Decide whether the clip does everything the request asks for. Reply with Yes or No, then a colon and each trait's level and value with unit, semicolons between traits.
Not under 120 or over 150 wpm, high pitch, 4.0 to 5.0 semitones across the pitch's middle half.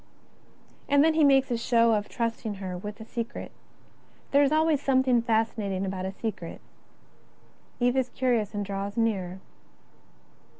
Yes: average, 145 wpm; high, 230 Hz; average, 4.3 semitones